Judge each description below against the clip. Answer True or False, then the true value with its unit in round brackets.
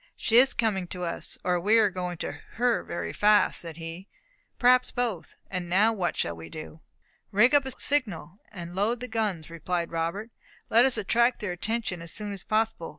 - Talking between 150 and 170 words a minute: False (195 wpm)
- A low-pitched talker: False (200 Hz)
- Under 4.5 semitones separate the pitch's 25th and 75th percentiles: False (4.8 semitones)